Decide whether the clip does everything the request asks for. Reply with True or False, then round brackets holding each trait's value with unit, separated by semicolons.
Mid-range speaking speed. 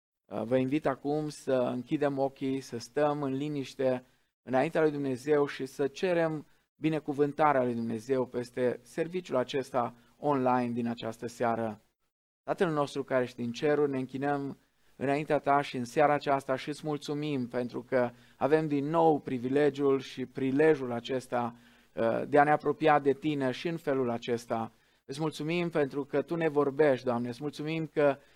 True (155 wpm)